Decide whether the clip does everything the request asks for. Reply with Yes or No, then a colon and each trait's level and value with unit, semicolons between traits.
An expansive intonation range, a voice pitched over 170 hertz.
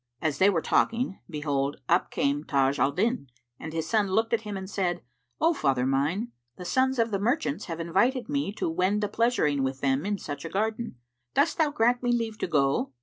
Yes: wide, 7.8 semitones; high, 190 Hz